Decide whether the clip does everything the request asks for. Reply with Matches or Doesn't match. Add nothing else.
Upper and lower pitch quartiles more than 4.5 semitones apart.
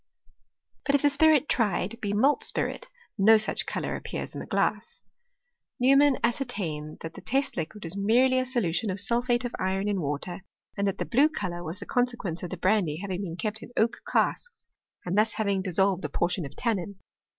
Matches